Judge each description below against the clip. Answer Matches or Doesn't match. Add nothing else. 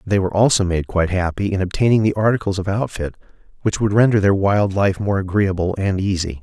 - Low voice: Matches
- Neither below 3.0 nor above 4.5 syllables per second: Doesn't match